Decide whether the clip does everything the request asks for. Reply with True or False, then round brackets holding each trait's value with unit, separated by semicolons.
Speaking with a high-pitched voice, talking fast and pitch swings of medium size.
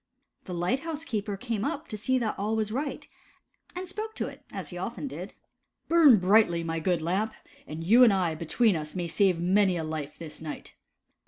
False (200 Hz; 210 wpm; 6.2 semitones)